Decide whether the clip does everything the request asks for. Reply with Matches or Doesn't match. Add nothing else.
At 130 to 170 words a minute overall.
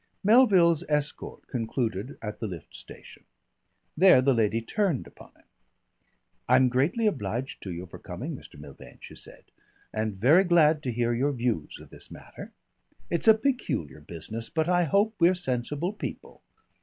Matches